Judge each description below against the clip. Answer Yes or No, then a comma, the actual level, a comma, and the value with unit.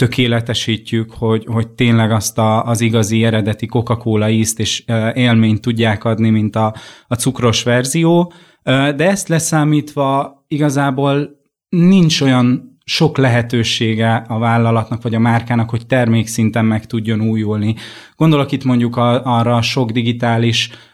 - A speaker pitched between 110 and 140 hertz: Yes, low, 120 Hz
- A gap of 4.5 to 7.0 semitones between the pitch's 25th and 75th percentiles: No, average, 2.7 semitones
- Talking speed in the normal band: Yes, average, 130 wpm